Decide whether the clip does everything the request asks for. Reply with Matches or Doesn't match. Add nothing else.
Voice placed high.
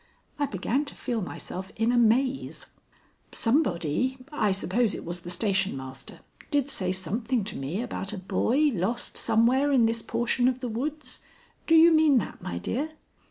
Matches